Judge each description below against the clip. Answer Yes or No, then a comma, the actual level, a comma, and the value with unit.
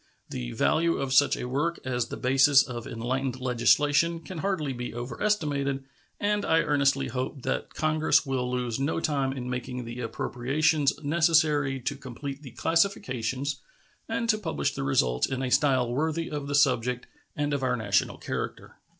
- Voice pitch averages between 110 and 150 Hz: Yes, low, 135 Hz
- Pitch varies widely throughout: No, average, 3.4 semitones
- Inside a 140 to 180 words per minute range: Yes, average, 165 wpm